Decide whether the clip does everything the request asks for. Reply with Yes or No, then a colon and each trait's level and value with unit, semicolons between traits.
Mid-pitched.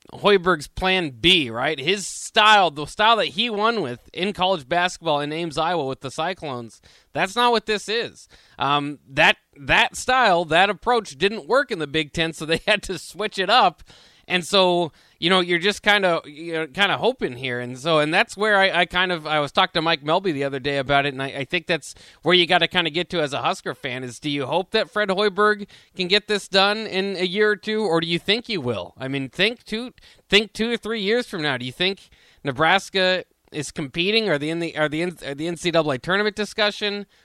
Yes: medium, 180 Hz